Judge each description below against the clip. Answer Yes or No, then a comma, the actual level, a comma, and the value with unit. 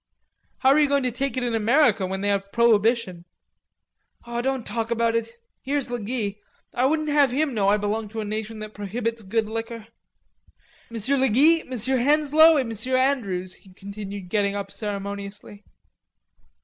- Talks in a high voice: Yes, high, 230 Hz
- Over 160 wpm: Yes, average, 170 wpm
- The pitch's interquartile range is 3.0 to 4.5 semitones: Yes, average, 4.2 semitones